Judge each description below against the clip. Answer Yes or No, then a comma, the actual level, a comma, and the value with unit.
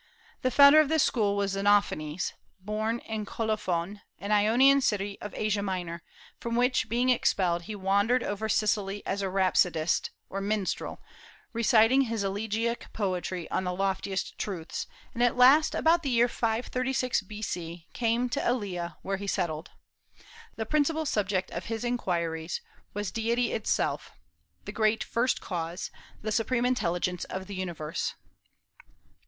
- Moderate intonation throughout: Yes, average, 3.9 semitones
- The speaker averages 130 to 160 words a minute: Yes, average, 145 wpm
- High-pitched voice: Yes, high, 210 Hz